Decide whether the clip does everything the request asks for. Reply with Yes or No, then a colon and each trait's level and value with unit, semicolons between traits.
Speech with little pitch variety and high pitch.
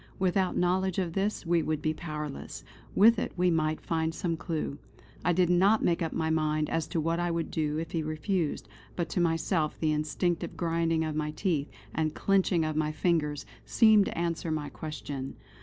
No: narrow, 2.3 semitones; medium, 165 Hz